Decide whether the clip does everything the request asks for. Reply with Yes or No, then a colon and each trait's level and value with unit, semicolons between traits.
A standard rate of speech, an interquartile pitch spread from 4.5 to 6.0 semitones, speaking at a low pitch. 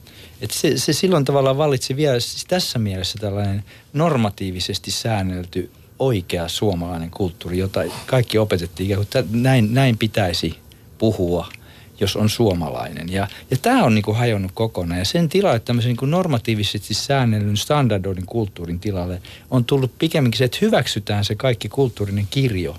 Yes: average, 145 wpm; average, 4.9 semitones; low, 110 Hz